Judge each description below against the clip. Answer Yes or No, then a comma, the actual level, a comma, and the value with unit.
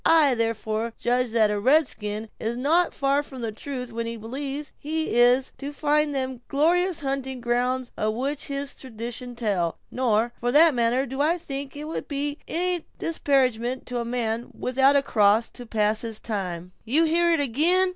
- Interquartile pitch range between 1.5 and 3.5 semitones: No, average, 3.9 semitones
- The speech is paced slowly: No, average, 185 wpm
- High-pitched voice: Yes, very high, 255 Hz